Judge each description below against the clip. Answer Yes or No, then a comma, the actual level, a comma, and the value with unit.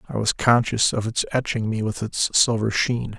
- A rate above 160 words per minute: Yes, fast, 205 wpm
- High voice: No, low, 115 Hz